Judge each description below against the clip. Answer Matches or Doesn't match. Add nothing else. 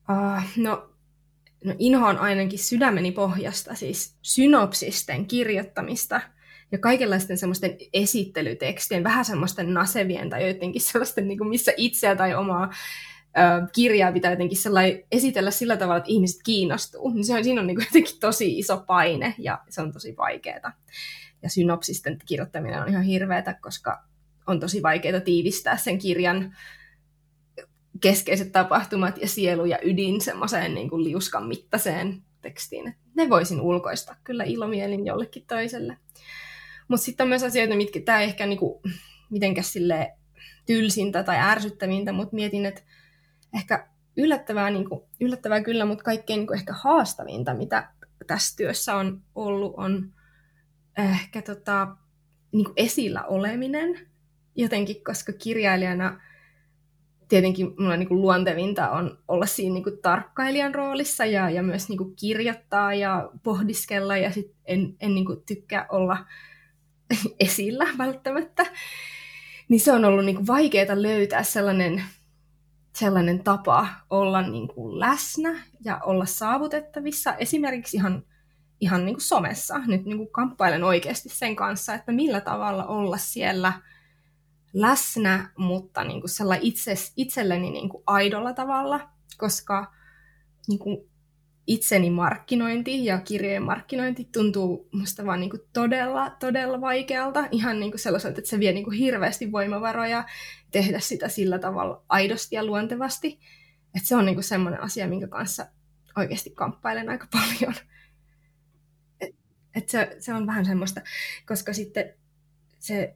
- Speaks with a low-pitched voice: Doesn't match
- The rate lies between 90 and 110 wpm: Doesn't match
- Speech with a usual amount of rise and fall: Matches